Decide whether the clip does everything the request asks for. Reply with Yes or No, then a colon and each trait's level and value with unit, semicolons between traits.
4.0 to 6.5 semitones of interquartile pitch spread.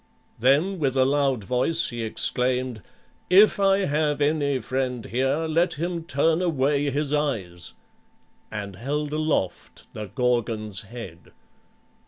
Yes: average, 4.4 semitones